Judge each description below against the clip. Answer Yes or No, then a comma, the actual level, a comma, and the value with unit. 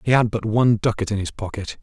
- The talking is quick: Yes, fast, 265 wpm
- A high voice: No, low, 110 Hz